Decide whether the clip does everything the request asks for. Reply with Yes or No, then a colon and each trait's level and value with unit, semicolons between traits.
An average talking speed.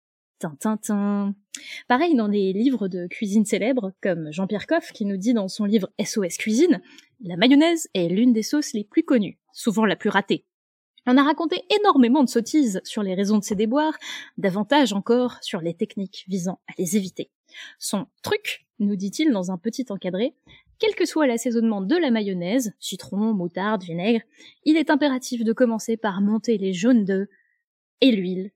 Yes: average, 175 wpm